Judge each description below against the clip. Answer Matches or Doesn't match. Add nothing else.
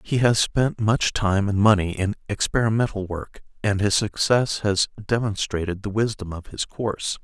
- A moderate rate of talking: Matches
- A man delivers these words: Matches